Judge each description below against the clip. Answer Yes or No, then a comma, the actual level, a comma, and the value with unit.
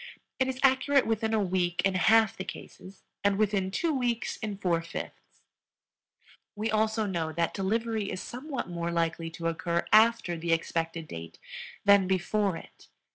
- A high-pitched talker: Yes, high, 195 Hz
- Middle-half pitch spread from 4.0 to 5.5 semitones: Yes, average, 4.6 semitones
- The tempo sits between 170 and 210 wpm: No, average, 160 wpm